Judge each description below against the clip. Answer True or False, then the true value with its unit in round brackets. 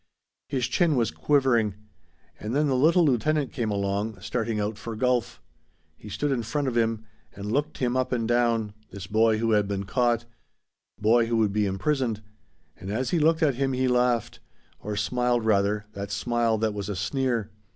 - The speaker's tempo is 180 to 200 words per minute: True (185 wpm)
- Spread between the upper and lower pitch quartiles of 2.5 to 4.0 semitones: True (3.5 semitones)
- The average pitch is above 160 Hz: False (115 Hz)